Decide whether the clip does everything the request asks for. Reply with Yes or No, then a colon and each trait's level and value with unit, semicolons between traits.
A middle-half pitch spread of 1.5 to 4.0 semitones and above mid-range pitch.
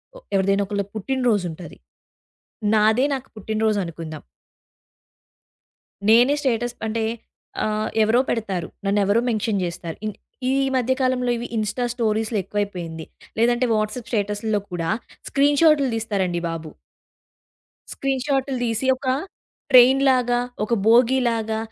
Yes: average, 3.6 semitones; high, 220 Hz